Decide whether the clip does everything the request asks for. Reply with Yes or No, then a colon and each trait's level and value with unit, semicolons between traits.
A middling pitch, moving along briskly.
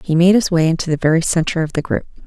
Yes: medium, 165 Hz; fast, 290 wpm